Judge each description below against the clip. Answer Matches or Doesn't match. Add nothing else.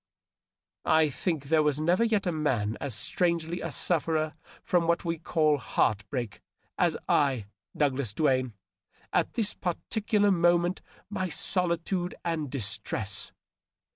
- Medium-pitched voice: Matches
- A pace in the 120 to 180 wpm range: Matches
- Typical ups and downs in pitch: Matches